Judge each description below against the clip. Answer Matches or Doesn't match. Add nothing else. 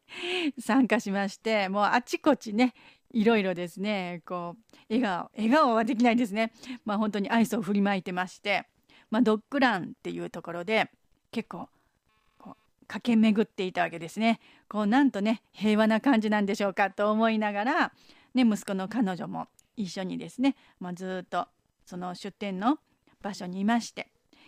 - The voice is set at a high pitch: Matches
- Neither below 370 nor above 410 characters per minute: Doesn't match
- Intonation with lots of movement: Doesn't match